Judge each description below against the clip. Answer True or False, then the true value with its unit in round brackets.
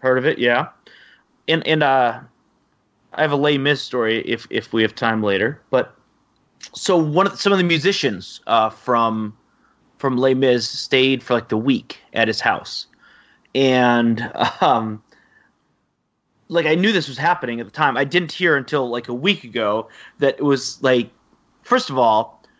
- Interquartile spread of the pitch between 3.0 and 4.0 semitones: False (4.7 semitones)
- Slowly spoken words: False (180 wpm)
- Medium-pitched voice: False (130 Hz)